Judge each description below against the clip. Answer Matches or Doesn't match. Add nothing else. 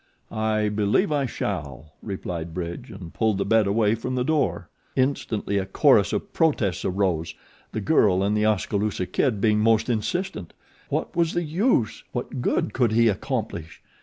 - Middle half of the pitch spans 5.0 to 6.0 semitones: Doesn't match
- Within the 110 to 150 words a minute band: Doesn't match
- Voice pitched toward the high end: Doesn't match